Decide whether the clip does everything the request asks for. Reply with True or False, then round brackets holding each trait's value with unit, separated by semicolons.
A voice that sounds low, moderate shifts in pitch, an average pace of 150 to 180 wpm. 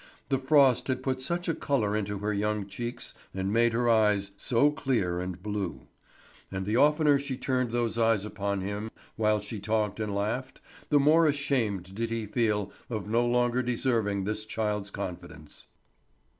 True (110 Hz; 3.9 semitones; 170 wpm)